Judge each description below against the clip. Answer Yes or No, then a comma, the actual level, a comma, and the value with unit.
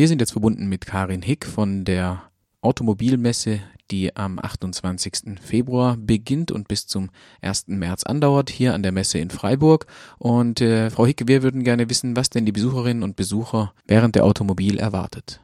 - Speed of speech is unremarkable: Yes, average, 175 wpm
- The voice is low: Yes, low, 110 Hz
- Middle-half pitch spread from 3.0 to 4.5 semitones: Yes, average, 4.0 semitones